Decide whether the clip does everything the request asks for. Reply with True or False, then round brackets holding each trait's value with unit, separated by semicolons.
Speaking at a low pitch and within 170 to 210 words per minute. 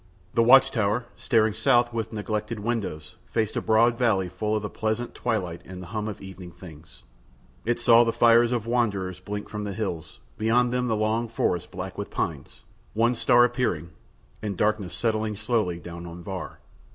True (110 Hz; 180 wpm)